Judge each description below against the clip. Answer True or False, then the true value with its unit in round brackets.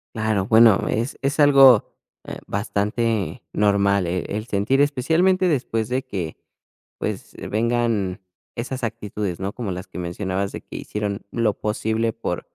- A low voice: True (110 Hz)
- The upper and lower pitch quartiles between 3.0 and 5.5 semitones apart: True (3.5 semitones)